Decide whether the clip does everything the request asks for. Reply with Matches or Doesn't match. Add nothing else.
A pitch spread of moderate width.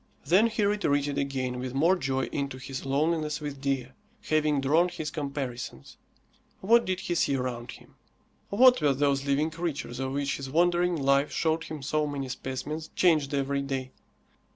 Matches